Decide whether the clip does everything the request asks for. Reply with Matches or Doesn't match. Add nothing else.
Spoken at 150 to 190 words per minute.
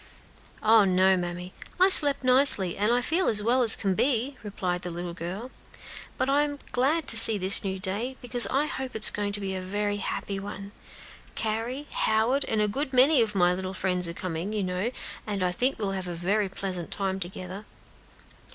Doesn't match